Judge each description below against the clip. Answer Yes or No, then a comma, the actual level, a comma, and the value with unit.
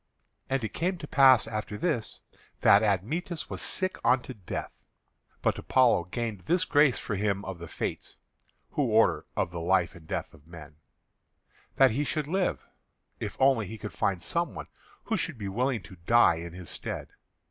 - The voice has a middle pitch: No, low, 110 Hz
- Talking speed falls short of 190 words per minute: Yes, average, 175 wpm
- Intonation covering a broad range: Yes, wide, 7.1 semitones